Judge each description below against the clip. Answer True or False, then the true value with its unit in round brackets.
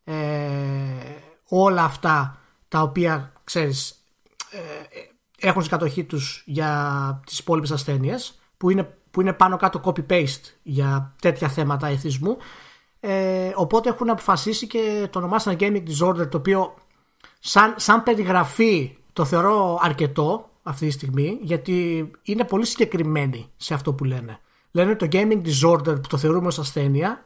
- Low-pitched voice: False (170 Hz)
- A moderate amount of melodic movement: True (4.7 semitones)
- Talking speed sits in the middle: True (140 wpm)